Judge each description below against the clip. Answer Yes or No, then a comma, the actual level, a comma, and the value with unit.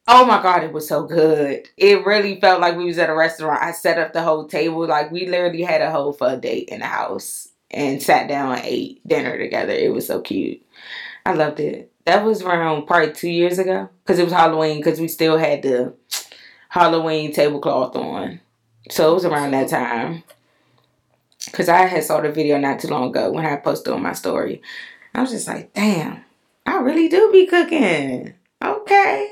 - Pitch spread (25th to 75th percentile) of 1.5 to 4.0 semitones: No, average, 4.5 semitones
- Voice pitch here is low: No, medium, 165 Hz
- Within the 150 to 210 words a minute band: Yes, fast, 205 wpm